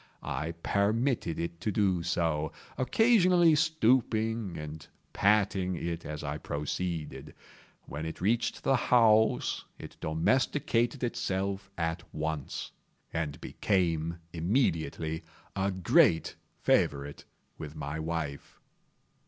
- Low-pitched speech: Yes, very low, 90 Hz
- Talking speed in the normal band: No, slow, 105 wpm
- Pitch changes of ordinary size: No, wide, 5.9 semitones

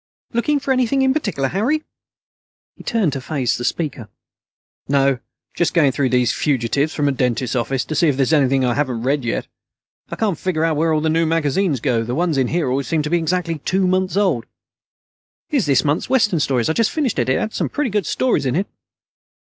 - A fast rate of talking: Yes, fast, 215 wpm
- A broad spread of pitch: Yes, wide, 6.0 semitones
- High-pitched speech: No, medium, 155 Hz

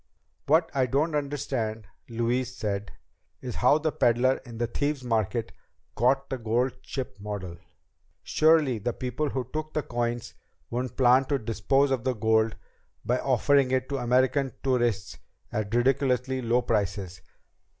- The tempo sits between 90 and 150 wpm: Yes, average, 145 wpm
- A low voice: Yes, low, 125 Hz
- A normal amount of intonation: Yes, average, 3.0 semitones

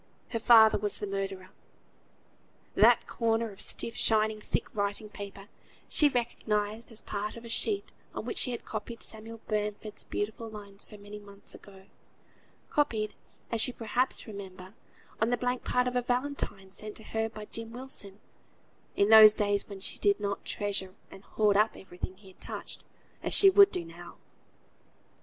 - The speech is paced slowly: No, average, 170 wpm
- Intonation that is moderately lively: No, narrow, 2.2 semitones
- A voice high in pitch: Yes, high, 215 Hz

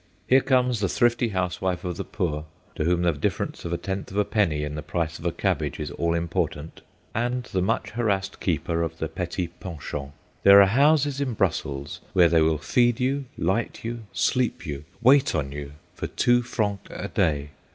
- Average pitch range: No, wide, 6.6 semitones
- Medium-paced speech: Yes, average, 195 wpm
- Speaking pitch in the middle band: No, very low, 90 Hz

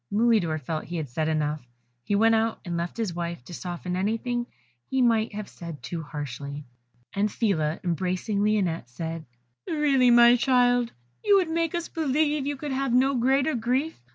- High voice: Yes, high, 215 Hz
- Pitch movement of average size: No, wide, 7.2 semitones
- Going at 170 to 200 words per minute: Yes, average, 175 wpm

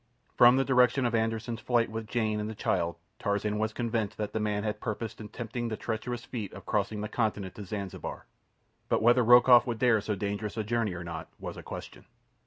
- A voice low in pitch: Yes, low, 110 Hz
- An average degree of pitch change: No, narrow, 2.2 semitones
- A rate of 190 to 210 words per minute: Yes, fast, 205 wpm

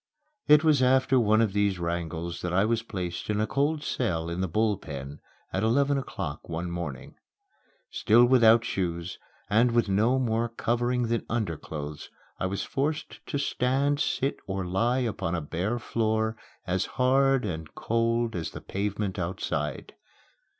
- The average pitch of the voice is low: Yes, low, 110 Hz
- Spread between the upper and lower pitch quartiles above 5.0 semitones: Yes, wide, 5.6 semitones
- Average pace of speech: Yes, average, 155 wpm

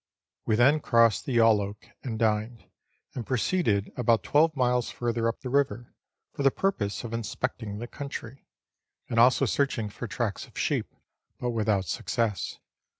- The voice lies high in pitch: No, low, 115 Hz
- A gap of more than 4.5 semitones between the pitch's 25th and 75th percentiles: No, average, 3.0 semitones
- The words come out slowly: No, average, 150 wpm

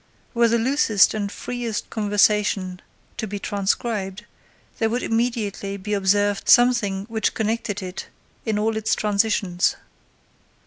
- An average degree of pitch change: No, narrow, 2.2 semitones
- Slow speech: Yes, slow, 125 wpm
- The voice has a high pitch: Yes, high, 210 Hz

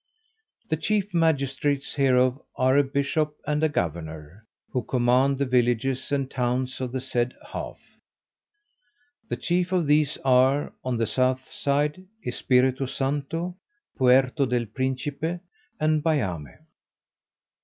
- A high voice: No, low, 135 Hz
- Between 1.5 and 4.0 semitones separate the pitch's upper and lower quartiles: Yes, average, 2.9 semitones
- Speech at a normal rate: No, slow, 120 wpm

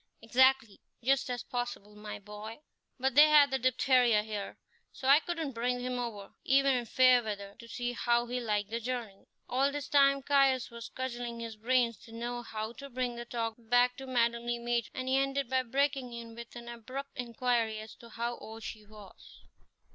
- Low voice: No, high, 240 Hz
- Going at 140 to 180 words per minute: No, average, 195 wpm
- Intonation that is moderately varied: No, narrow, 2.3 semitones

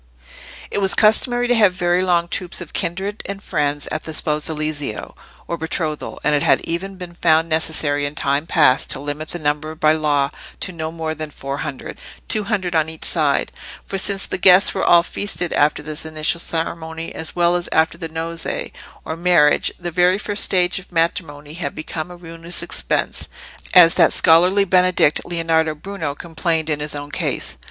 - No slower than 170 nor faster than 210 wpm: Yes, average, 180 wpm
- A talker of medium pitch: Yes, medium, 165 Hz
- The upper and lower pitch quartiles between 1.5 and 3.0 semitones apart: Yes, average, 2.7 semitones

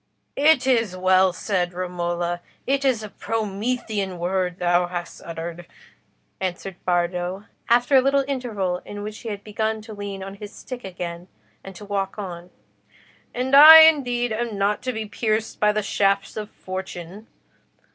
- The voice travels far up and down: No, average, 4.0 semitones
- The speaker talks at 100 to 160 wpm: Yes, average, 155 wpm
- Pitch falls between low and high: No, high, 200 Hz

